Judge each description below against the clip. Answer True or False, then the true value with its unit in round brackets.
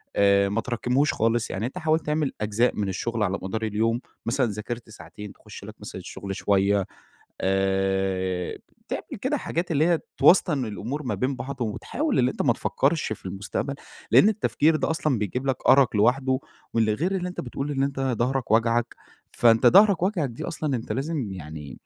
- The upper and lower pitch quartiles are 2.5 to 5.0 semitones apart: False (5.5 semitones)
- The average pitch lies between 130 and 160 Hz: False (120 Hz)